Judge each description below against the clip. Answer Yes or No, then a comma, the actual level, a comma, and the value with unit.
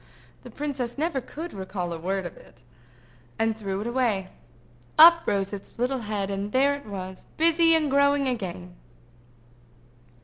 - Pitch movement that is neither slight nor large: No, wide, 6.9 semitones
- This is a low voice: No, high, 210 Hz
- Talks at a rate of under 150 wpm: Yes, average, 140 wpm